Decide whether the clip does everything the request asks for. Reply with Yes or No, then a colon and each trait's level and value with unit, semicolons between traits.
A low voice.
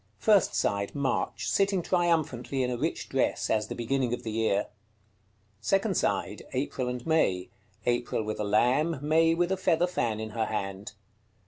Yes: low, 125 Hz